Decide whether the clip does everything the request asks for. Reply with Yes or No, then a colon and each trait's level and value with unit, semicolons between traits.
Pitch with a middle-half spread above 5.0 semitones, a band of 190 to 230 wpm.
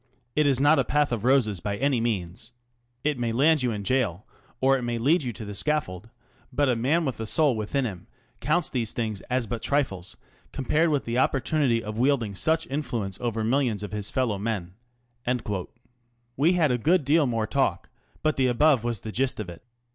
No: average, 4.6 semitones; fast, 205 wpm